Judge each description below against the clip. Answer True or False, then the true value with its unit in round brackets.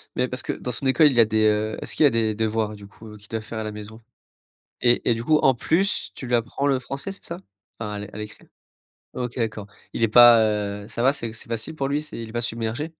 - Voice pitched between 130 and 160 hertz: False (115 Hz)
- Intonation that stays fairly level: False (3.2 semitones)